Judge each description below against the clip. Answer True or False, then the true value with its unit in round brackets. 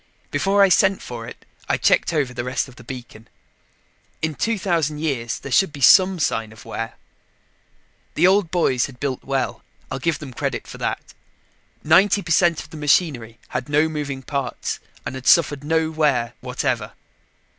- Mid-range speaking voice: True (145 Hz)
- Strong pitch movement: False (4.7 semitones)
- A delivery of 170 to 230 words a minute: True (175 wpm)